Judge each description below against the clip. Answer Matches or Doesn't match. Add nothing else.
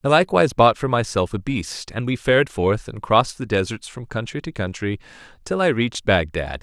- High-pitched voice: Doesn't match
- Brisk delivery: Matches